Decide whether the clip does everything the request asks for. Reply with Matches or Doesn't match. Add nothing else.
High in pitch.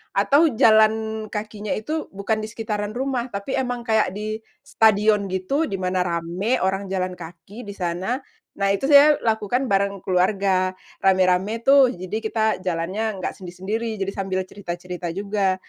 Matches